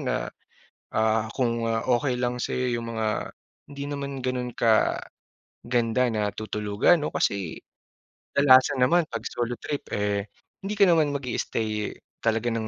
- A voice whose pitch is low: Yes, low, 120 Hz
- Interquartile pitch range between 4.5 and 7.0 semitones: No, average, 3.6 semitones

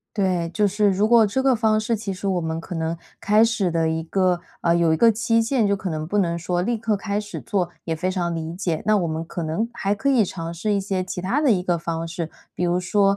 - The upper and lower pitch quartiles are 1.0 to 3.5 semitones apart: No, average, 4.0 semitones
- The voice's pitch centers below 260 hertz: Yes, high, 190 Hz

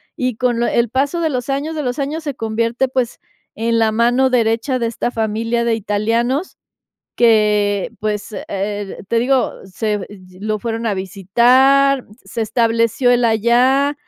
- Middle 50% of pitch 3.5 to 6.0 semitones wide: No, average, 2.9 semitones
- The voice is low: No, high, 235 Hz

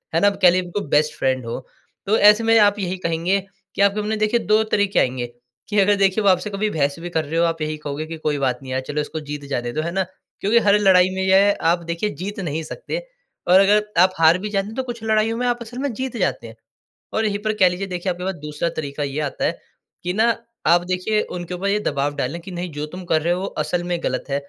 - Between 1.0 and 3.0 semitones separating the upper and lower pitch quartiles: No, average, 4.8 semitones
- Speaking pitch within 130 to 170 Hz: No, medium, 185 Hz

